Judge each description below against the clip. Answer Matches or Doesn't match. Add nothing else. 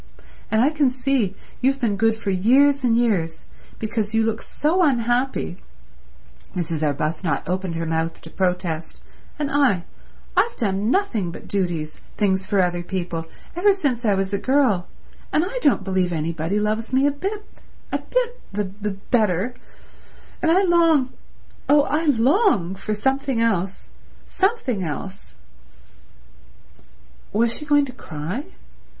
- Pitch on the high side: Matches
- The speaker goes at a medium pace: Doesn't match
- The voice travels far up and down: Matches